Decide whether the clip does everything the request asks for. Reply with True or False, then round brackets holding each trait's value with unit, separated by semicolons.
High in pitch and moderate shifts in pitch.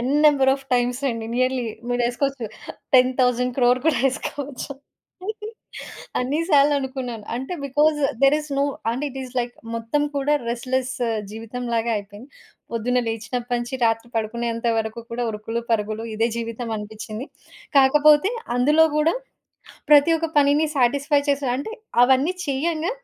True (250 Hz; 3.3 semitones)